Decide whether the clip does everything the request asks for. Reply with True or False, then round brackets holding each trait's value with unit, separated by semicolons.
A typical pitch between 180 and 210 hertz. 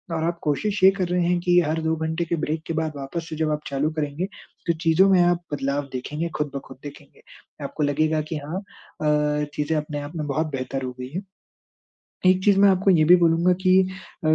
False (160 Hz)